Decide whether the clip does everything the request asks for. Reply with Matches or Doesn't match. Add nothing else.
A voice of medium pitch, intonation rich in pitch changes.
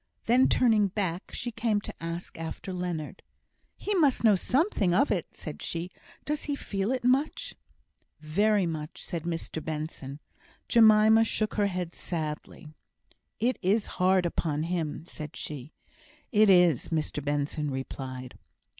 Matches